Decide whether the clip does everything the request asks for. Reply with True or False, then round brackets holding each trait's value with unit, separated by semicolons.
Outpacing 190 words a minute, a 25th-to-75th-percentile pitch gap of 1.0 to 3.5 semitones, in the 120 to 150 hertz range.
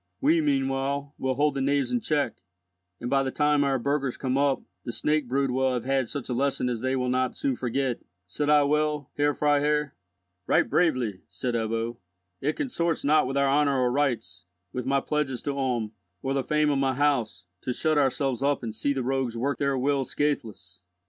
True (200 wpm; 2.4 semitones; 135 Hz)